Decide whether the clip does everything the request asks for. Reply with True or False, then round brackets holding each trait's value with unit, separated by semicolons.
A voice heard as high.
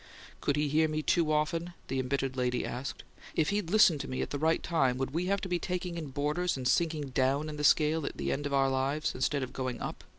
False (150 Hz)